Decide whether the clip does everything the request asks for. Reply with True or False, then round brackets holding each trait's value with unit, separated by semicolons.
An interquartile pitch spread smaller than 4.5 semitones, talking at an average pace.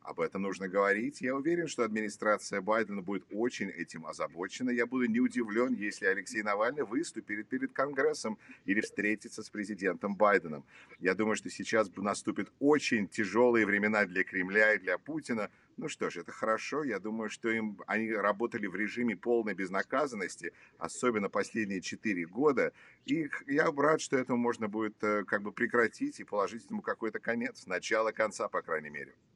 True (2.7 semitones; 165 wpm)